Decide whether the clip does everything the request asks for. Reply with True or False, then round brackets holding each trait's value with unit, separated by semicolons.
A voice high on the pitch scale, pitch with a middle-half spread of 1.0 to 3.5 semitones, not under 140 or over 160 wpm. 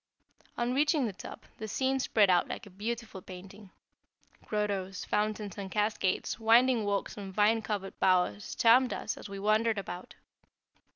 True (210 Hz; 2.8 semitones; 155 wpm)